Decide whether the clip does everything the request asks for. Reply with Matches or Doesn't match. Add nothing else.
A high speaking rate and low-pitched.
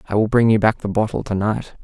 Matches